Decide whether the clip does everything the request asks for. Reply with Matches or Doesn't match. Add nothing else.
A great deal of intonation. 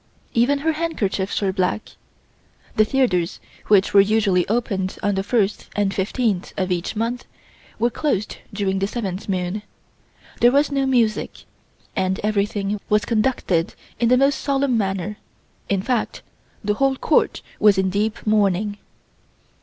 Doesn't match